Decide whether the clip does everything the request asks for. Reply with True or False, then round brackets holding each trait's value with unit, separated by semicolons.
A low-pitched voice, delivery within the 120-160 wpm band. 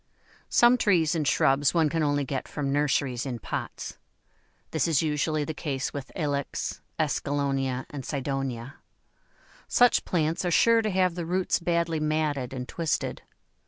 False (150 Hz; 150 wpm)